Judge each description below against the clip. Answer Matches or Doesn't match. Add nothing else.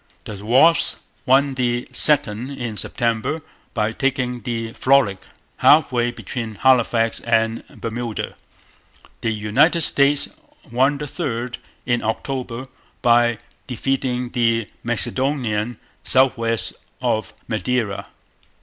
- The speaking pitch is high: Doesn't match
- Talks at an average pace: Doesn't match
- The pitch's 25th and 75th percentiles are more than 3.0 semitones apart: Doesn't match